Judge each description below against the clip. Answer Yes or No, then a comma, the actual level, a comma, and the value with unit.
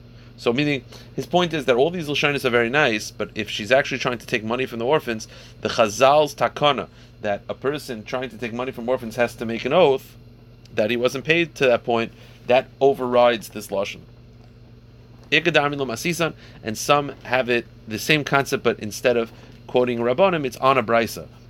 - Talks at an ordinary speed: Yes, average, 180 wpm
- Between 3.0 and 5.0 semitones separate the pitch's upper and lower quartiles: No, narrow, 2.4 semitones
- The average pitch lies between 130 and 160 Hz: No, low, 120 Hz